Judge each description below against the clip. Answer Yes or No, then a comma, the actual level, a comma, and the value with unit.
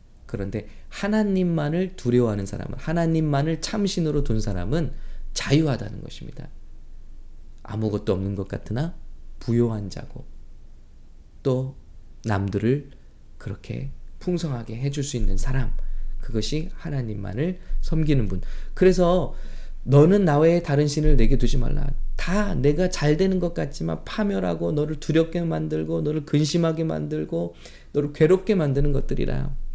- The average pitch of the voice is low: Yes, low, 130 Hz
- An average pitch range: No, wide, 8.4 semitones